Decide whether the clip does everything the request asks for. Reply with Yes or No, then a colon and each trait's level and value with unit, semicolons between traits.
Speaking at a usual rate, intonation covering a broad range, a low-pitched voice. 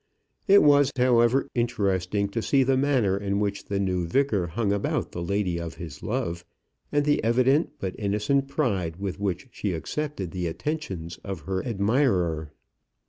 Yes: average, 160 wpm; wide, 6.3 semitones; low, 100 Hz